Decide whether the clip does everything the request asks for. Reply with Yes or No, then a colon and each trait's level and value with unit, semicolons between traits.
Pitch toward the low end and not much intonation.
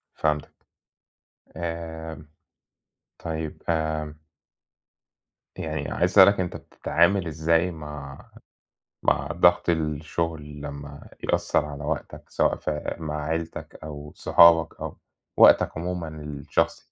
Yes: very low, 80 Hz; narrow, 1.8 semitones